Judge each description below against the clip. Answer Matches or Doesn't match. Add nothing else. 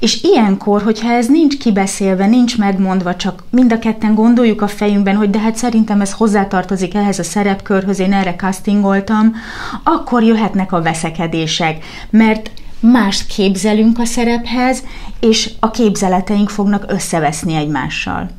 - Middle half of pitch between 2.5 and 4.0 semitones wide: Matches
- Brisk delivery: Doesn't match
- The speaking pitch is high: Matches